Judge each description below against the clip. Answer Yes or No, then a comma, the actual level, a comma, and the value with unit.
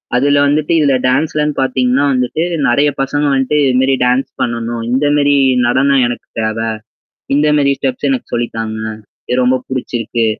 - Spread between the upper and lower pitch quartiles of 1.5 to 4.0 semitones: Yes, average, 3.1 semitones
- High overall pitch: No, low, 130 Hz